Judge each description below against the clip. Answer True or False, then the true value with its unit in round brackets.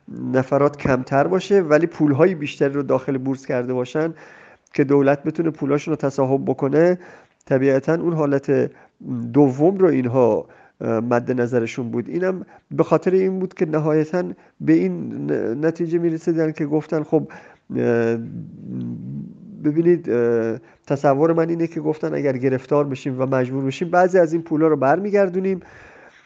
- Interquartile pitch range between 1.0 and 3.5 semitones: False (4.0 semitones)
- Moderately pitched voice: True (150 Hz)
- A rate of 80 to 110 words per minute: False (135 wpm)